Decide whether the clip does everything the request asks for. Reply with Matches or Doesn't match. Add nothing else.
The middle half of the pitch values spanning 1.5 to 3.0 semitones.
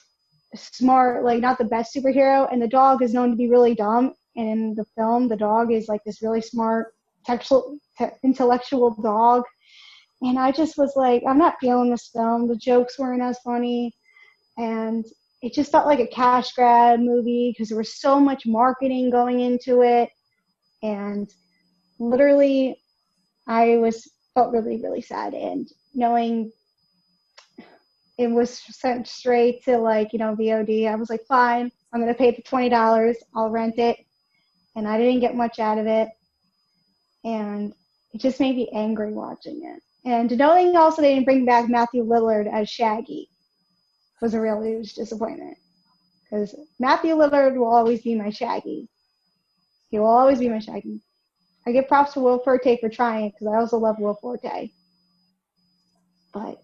Matches